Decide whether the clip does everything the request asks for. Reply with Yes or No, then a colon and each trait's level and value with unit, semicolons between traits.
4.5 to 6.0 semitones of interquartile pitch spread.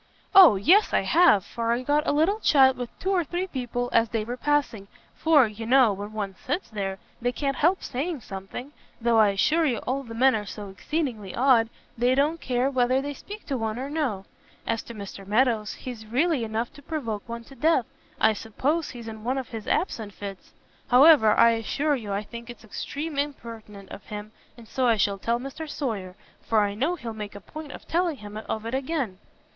Yes: average, 4.9 semitones